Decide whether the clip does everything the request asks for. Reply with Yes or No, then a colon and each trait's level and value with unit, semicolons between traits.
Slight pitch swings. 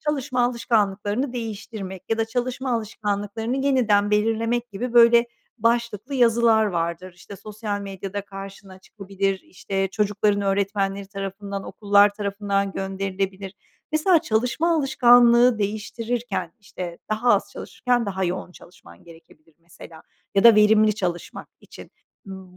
No: average, 3.3 semitones